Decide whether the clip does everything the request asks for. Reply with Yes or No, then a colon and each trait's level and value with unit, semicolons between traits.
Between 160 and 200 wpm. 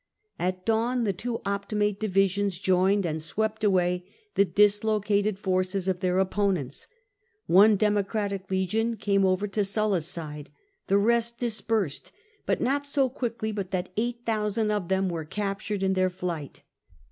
No: average, 145 wpm